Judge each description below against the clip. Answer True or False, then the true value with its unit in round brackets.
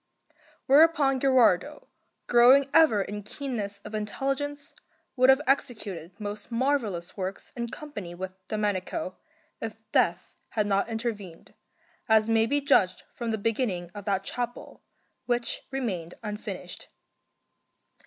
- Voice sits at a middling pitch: False (220 Hz)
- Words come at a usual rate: False (120 wpm)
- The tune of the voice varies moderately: True (4.9 semitones)